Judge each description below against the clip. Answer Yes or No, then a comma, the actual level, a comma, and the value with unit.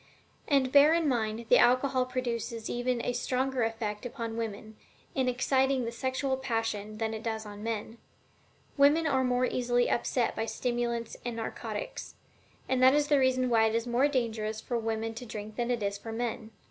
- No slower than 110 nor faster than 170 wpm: No, average, 185 wpm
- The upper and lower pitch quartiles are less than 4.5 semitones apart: Yes, narrow, 2.5 semitones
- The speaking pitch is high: Yes, high, 240 Hz